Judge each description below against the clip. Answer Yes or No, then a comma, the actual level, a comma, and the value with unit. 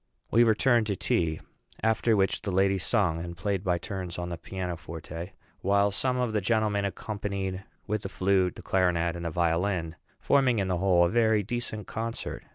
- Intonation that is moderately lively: Yes, average, 3.5 semitones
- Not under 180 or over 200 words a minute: Yes, average, 185 wpm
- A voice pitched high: No, very low, 95 Hz